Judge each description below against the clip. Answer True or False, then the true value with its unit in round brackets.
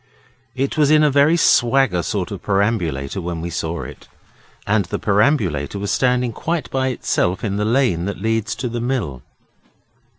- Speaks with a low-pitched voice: True (110 Hz)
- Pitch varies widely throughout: True (6.7 semitones)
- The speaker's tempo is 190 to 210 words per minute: False (170 wpm)